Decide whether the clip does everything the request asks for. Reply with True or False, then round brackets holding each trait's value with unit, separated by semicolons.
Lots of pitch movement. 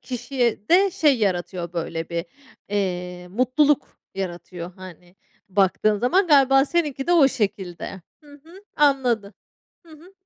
True (7.9 semitones)